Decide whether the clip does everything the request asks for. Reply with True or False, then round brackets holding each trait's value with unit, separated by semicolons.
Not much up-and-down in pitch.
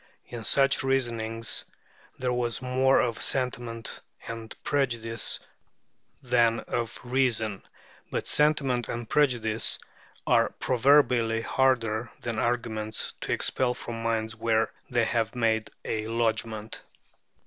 True (2.0 semitones)